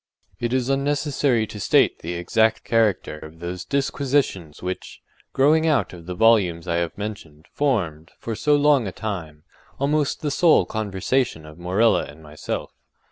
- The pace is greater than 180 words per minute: No, average, 155 wpm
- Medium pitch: No, low, 105 Hz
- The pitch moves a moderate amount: No, wide, 8.0 semitones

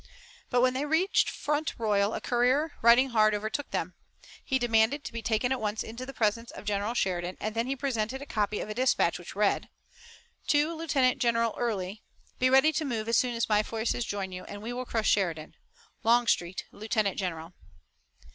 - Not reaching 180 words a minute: No, average, 195 wpm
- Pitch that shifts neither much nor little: Yes, average, 3.6 semitones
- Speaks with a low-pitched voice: No, high, 230 Hz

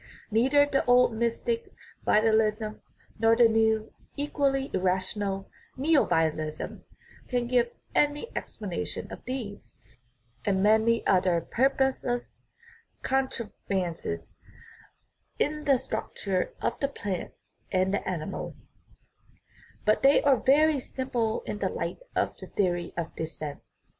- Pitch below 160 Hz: No, high, 225 Hz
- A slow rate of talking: Yes, slow, 110 wpm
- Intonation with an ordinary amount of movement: No, wide, 5.8 semitones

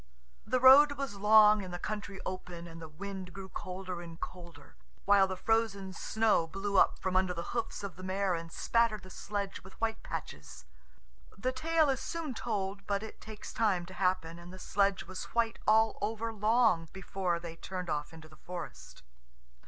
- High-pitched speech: Yes, high, 195 Hz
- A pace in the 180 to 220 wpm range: Yes, average, 185 wpm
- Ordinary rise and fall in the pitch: Yes, average, 3.6 semitones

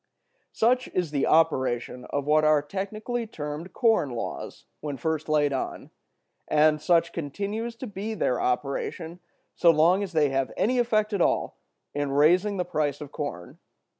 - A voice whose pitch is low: No, medium, 160 Hz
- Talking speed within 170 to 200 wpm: No, average, 160 wpm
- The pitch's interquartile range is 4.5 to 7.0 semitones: Yes, wide, 5.6 semitones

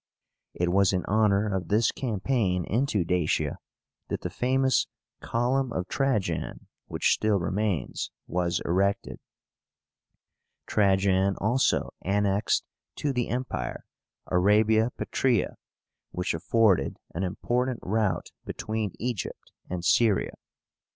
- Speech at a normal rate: No, slow, 105 wpm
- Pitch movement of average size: Yes, average, 4.2 semitones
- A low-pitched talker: Yes, low, 105 Hz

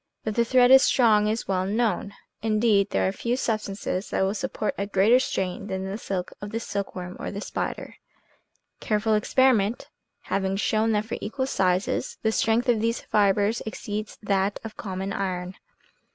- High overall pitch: Yes, high, 210 Hz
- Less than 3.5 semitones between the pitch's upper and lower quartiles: Yes, narrow, 2.6 semitones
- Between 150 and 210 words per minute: Yes, average, 170 wpm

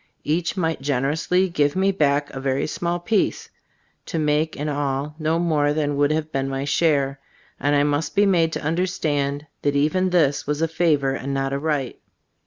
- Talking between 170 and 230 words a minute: Yes, average, 190 wpm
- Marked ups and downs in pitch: No, narrow, 2.6 semitones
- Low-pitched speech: No, medium, 150 Hz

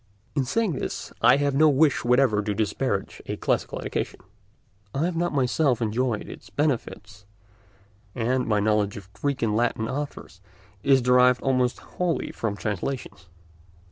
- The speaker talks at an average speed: Yes, average, 145 wpm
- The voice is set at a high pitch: No, low, 125 Hz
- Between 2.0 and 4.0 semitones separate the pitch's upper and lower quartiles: No, average, 4.5 semitones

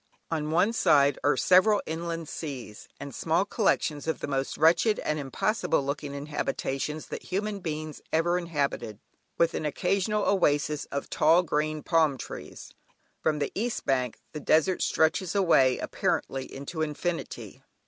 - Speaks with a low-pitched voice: No, medium, 155 Hz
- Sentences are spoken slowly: No, average, 145 wpm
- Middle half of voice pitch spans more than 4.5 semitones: No, average, 3.7 semitones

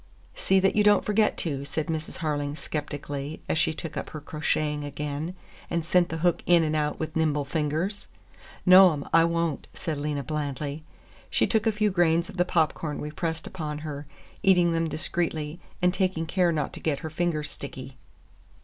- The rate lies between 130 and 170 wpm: No, average, 185 wpm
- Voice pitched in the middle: Yes, medium, 160 Hz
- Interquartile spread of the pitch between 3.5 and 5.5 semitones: No, average, 2.8 semitones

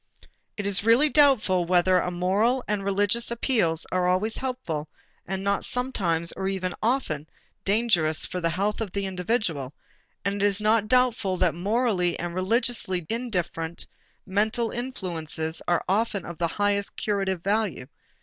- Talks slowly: No, average, 150 wpm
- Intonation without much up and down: No, average, 4.3 semitones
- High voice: Yes, high, 195 Hz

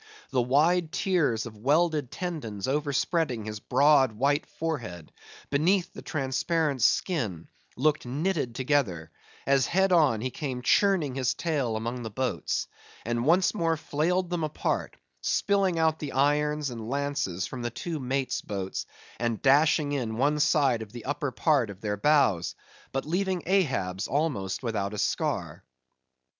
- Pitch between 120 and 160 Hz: Yes, medium, 140 Hz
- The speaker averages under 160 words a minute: Yes, average, 150 wpm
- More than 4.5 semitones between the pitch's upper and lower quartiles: Yes, average, 5.2 semitones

